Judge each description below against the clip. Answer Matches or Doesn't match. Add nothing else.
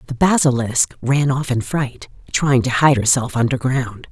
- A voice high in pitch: Doesn't match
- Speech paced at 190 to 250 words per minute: Doesn't match